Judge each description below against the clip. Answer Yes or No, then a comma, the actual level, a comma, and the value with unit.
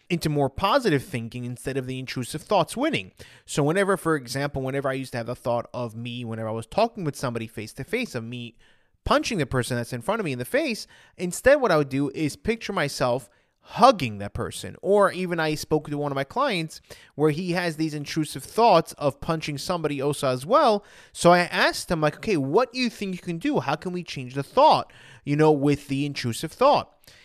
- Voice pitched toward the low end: No, medium, 145 Hz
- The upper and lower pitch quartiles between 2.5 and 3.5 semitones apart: No, wide, 5.5 semitones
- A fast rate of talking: Yes, fast, 225 wpm